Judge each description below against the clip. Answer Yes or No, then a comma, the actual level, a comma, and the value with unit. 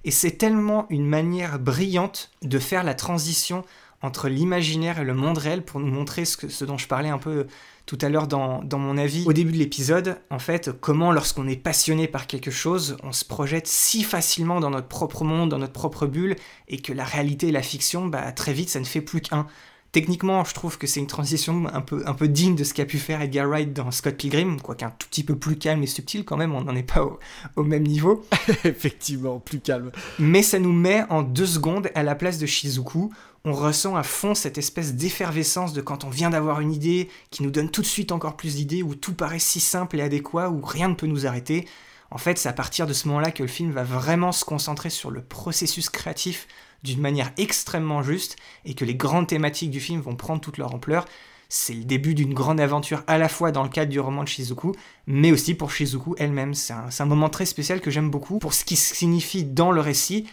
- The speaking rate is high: Yes, fast, 240 wpm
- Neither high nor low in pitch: Yes, medium, 155 Hz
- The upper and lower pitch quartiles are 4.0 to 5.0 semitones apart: No, average, 3.4 semitones